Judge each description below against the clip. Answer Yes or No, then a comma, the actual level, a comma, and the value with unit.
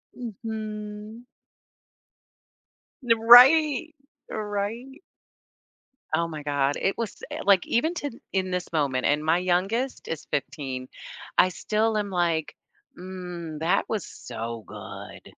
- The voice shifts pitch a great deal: Yes, wide, 6.1 semitones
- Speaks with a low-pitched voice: No, high, 195 Hz